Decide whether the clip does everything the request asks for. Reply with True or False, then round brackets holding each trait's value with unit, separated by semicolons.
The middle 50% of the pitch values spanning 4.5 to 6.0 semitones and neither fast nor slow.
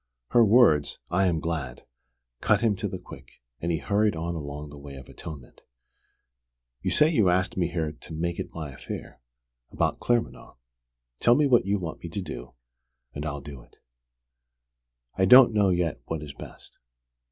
True (5.5 semitones; 175 wpm)